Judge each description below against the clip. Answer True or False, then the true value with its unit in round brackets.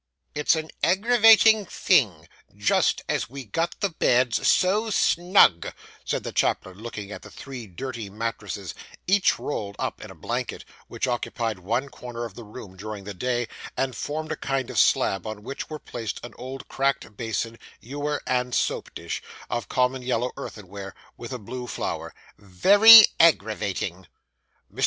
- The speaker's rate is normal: True (155 wpm)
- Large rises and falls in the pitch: True (5.7 semitones)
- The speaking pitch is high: False (125 Hz)